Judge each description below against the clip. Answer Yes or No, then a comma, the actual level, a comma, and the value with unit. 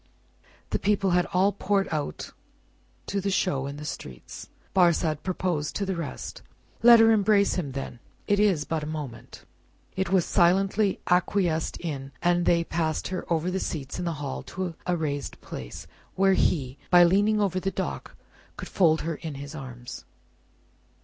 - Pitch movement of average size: Yes, average, 4.2 semitones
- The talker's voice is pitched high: No, medium, 175 Hz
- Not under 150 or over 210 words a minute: Yes, average, 170 wpm